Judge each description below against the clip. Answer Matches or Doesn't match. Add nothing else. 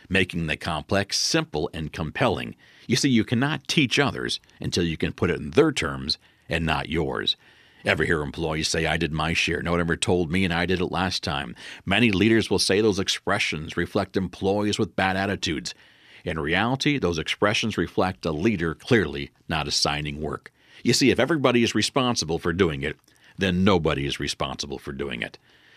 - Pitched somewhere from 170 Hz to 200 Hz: Doesn't match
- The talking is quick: Doesn't match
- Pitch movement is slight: Doesn't match